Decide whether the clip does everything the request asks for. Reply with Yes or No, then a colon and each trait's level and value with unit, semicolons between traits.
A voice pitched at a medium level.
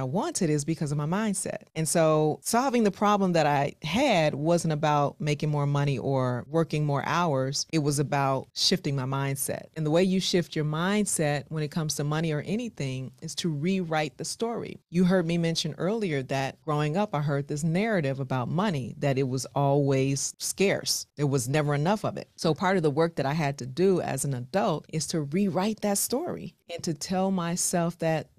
Yes: medium, 160 Hz